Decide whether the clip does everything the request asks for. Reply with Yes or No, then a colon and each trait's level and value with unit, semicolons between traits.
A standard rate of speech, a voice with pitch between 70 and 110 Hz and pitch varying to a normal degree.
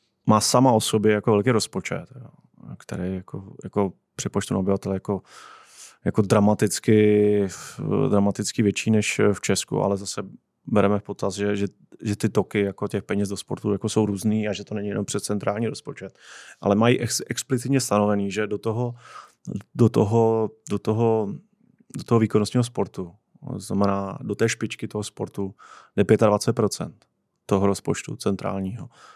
No: average, 150 wpm; low, 105 Hz; narrow, 1.7 semitones